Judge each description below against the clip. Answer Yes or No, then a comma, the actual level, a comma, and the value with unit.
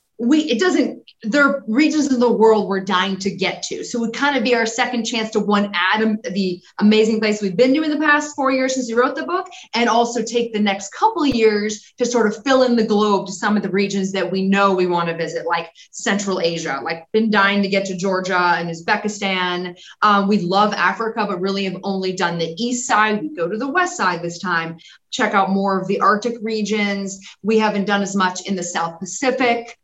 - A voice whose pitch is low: No, high, 210 Hz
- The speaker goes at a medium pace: No, fast, 235 wpm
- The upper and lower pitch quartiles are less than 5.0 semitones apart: Yes, average, 3.9 semitones